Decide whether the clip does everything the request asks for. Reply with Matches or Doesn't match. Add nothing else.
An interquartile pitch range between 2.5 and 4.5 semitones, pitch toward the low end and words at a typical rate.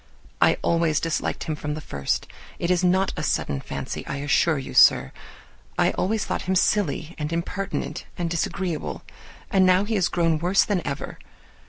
Doesn't match